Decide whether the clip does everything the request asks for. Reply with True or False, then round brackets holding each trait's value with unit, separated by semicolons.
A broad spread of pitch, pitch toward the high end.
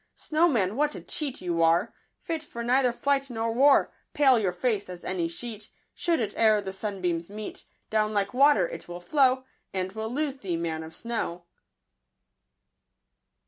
True (6.3 semitones; 215 Hz)